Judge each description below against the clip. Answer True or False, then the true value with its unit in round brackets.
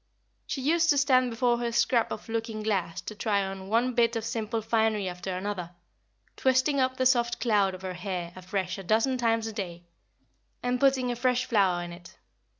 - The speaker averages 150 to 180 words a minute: False (195 wpm)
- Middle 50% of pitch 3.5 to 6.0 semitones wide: True (4.6 semitones)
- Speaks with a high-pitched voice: True (225 Hz)